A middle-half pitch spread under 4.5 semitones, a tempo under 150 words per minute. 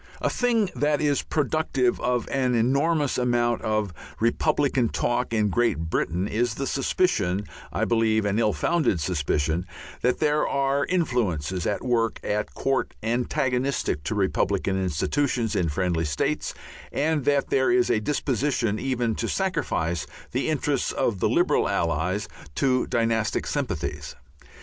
No: wide, 5.4 semitones; average, 140 wpm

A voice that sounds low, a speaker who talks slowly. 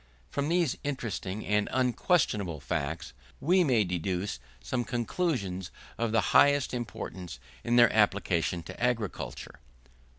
Yes: low, 110 Hz; slow, 120 wpm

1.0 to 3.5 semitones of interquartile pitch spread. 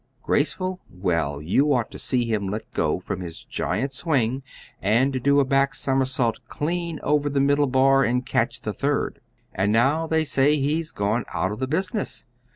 No: average, 4.5 semitones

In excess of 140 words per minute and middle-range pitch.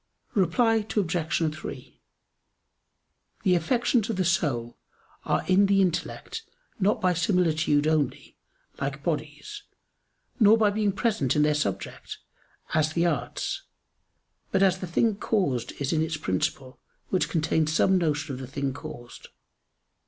No: slow, 135 wpm; medium, 165 Hz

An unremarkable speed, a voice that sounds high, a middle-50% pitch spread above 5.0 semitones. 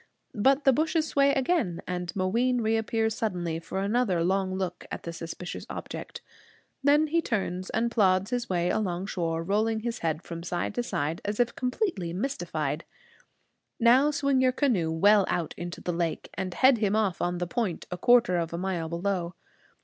Yes: average, 180 wpm; high, 195 Hz; wide, 5.6 semitones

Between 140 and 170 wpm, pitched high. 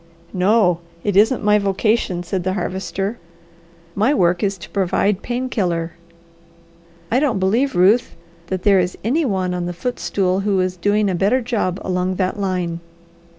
Yes: average, 160 wpm; high, 195 Hz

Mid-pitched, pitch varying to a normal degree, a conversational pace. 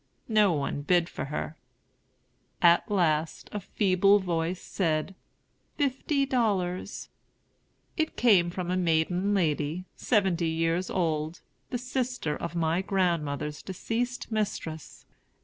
No: medium, 180 Hz; average, 4.1 semitones; slow, 115 wpm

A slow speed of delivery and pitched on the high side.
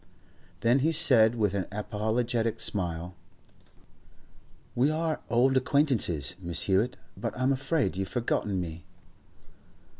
No: slow, 115 wpm; low, 115 Hz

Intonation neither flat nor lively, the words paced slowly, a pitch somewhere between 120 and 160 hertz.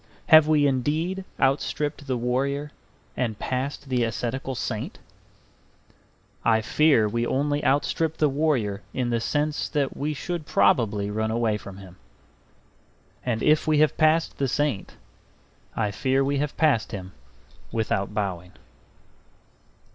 Yes: average, 5.0 semitones; slow, 130 wpm; low, 135 Hz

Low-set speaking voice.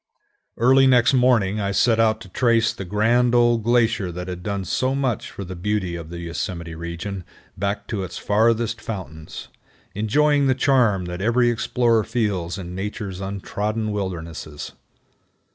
Yes: low, 105 Hz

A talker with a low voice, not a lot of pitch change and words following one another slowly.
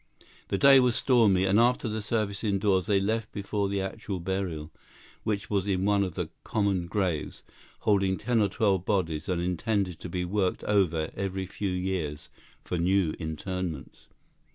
No: very low, 95 Hz; narrow, 2.3 semitones; average, 165 wpm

